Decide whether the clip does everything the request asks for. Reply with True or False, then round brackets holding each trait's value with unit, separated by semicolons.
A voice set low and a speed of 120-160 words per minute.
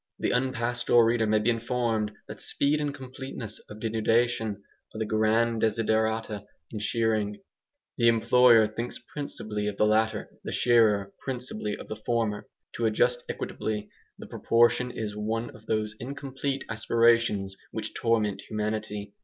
True (110 Hz; 140 wpm)